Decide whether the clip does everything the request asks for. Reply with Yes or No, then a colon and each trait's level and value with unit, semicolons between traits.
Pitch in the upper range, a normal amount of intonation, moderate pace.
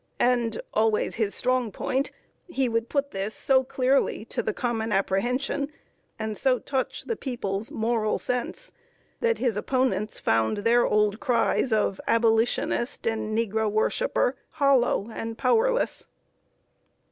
No: high, 230 Hz; average, 3.4 semitones; slow, 130 wpm